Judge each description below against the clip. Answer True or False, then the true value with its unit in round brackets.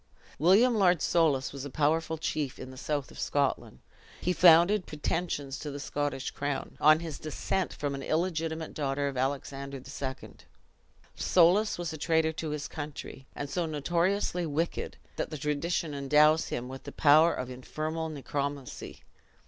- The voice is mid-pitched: True (150 Hz)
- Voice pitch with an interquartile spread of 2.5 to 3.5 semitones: True (2.9 semitones)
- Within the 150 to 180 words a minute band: True (155 wpm)